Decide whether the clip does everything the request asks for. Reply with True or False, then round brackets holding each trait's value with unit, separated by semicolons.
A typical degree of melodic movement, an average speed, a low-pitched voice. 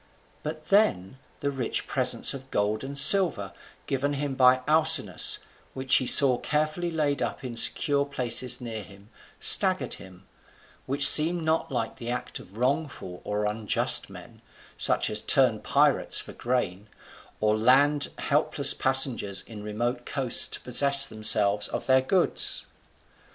True (4.8 semitones; 145 wpm; 130 Hz)